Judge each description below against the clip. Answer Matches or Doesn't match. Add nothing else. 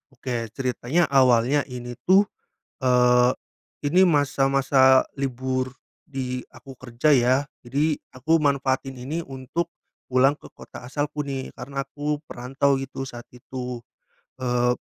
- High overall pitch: Doesn't match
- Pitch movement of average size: Doesn't match